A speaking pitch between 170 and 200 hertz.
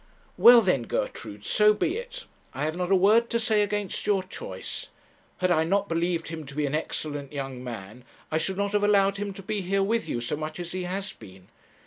Yes: medium, 185 Hz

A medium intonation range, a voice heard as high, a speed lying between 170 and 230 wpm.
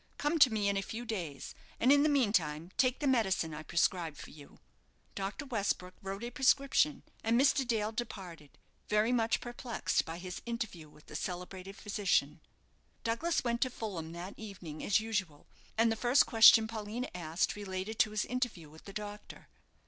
Yes: average, 4.8 semitones; high, 210 Hz; average, 175 wpm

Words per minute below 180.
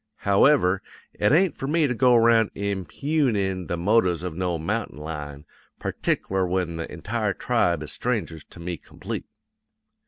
Yes: average, 150 wpm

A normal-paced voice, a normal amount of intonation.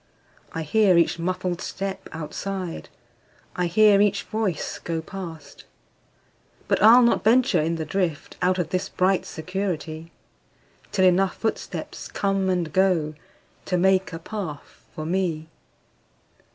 No: slow, 110 wpm; average, 3.1 semitones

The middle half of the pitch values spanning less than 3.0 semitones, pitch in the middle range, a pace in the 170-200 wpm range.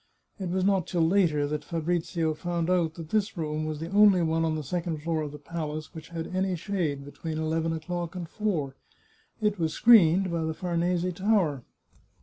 Yes: narrow, 2.6 semitones; medium, 165 Hz; average, 190 wpm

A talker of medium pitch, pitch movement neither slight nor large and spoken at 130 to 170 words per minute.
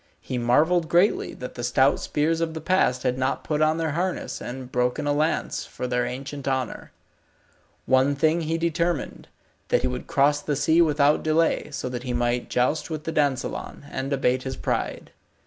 No: medium, 145 Hz; average, 3.9 semitones; average, 185 wpm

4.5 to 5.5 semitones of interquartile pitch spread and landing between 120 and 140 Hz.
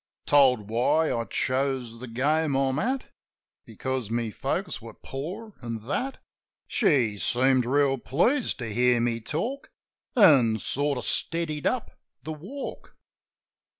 Yes: average, 4.9 semitones; low, 135 Hz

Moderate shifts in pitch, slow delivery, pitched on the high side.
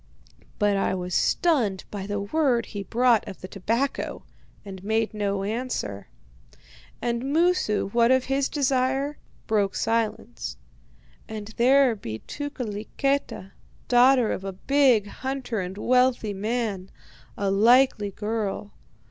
Yes: average, 4.5 semitones; slow, 125 wpm; high, 225 Hz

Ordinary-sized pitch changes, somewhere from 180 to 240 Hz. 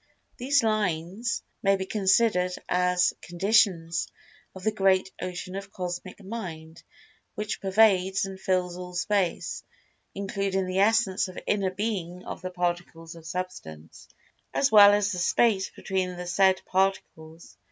No: narrow, 2.1 semitones; high, 190 Hz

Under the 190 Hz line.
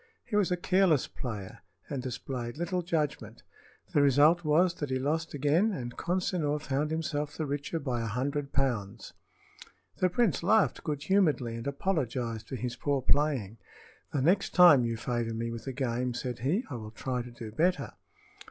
Yes: medium, 140 Hz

